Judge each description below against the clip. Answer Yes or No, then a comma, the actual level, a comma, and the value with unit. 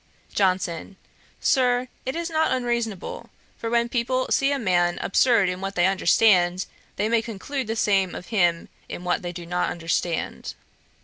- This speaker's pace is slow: No, average, 165 wpm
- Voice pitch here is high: Yes, high, 200 Hz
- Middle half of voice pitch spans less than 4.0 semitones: No, wide, 5.4 semitones